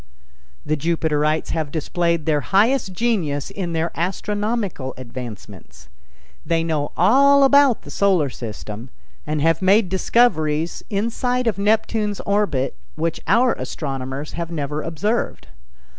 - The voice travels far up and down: Yes, wide, 5.9 semitones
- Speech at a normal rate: No, slow, 120 wpm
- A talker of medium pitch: Yes, medium, 170 Hz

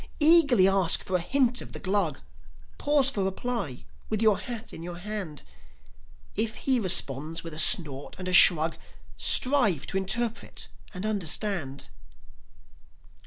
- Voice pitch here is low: No, high, 195 Hz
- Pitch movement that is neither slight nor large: No, wide, 5.7 semitones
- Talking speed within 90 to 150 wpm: Yes, average, 140 wpm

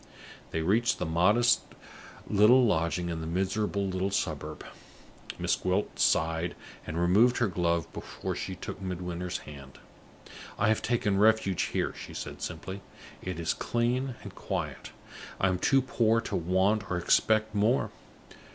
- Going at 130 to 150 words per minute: Yes, average, 145 wpm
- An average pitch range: Yes, average, 4.2 semitones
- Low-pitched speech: Yes, very low, 95 Hz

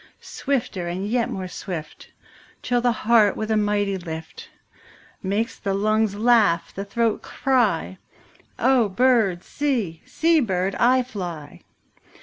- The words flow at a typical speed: No, slow, 130 wpm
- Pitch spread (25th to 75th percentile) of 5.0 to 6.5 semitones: No, average, 4.4 semitones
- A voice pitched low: No, high, 210 Hz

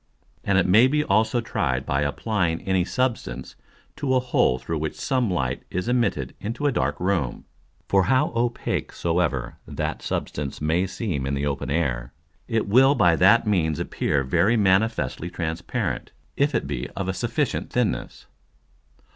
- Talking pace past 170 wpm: No, average, 160 wpm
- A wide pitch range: Yes, wide, 6.9 semitones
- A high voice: No, very low, 95 Hz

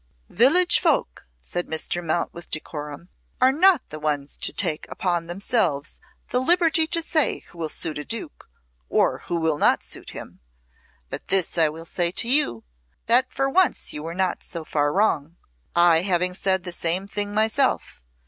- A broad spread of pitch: Yes, wide, 7.1 semitones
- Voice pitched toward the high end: No, medium, 175 Hz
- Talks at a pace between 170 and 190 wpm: Yes, average, 175 wpm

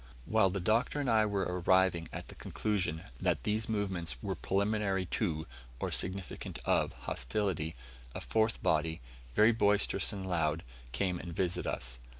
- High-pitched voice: No, very low, 95 Hz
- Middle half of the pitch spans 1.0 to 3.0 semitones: No, average, 4.0 semitones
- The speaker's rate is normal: Yes, average, 155 wpm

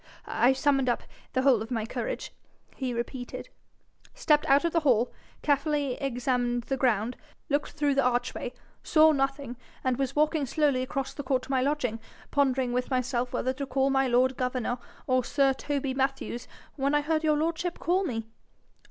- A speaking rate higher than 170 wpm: Yes, average, 180 wpm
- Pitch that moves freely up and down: No, narrow, 2.5 semitones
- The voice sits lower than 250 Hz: No, very high, 270 Hz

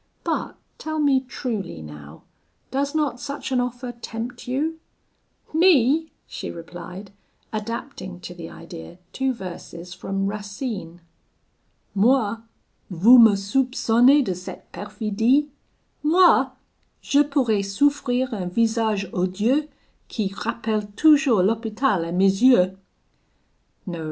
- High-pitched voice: Yes, high, 225 Hz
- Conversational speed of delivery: No, slow, 110 wpm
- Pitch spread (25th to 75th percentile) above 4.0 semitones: Yes, wide, 5.6 semitones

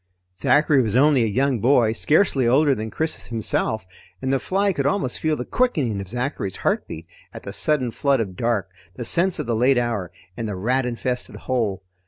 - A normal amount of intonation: Yes, average, 4.2 semitones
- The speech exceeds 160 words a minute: Yes, average, 195 wpm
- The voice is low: Yes, low, 125 Hz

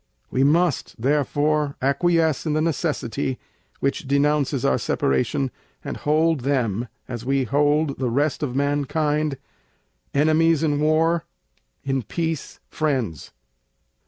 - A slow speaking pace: Yes, slow, 115 wpm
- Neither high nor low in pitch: Yes, medium, 145 Hz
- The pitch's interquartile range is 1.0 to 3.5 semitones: Yes, narrow, 2.6 semitones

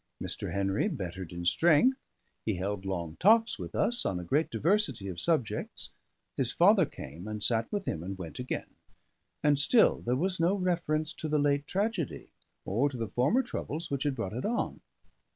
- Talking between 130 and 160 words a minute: No, average, 185 wpm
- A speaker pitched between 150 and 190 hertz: No, medium, 140 Hz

